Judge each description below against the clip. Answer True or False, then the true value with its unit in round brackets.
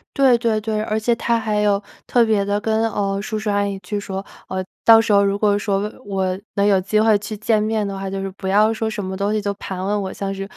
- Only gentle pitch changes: True (1.7 semitones)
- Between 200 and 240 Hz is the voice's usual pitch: True (205 Hz)